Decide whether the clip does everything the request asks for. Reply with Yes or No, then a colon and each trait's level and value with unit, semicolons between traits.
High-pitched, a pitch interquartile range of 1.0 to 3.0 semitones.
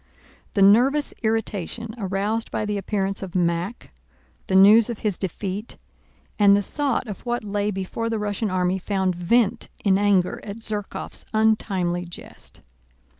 Yes: high, 205 Hz; narrow, 2.6 semitones